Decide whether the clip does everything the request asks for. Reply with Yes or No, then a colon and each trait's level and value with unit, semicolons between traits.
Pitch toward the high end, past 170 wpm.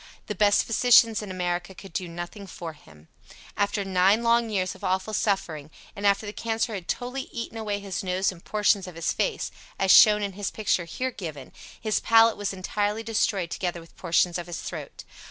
Yes: high, 200 Hz; average, 195 wpm